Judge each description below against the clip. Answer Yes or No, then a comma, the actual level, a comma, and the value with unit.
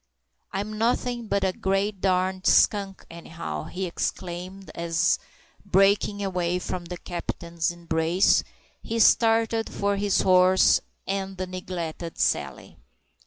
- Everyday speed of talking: No, slow, 120 wpm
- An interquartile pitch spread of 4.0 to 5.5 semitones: No, narrow, 2.5 semitones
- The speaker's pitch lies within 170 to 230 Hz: Yes, medium, 185 Hz